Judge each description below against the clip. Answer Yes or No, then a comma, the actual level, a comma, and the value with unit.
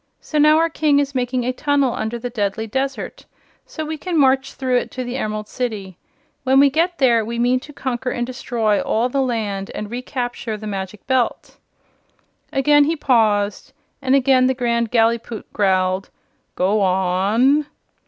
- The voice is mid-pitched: No, high, 245 Hz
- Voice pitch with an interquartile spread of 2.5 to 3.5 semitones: No, average, 3.9 semitones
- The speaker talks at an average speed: Yes, average, 170 wpm